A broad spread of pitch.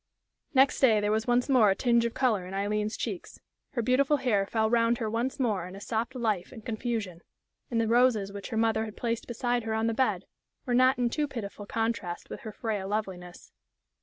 No: average, 2.7 semitones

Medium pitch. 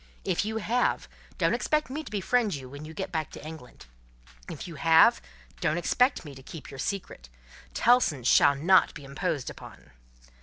Yes: medium, 165 Hz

